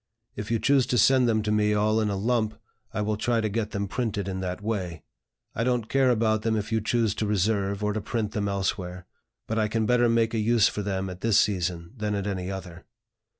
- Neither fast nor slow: No, fast, 235 wpm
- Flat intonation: Yes, narrow, 2.3 semitones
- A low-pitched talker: Yes, low, 105 Hz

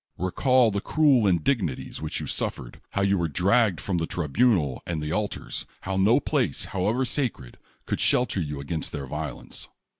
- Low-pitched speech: Yes, very low, 95 Hz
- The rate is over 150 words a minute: Yes, average, 170 wpm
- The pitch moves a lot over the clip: Yes, wide, 6.7 semitones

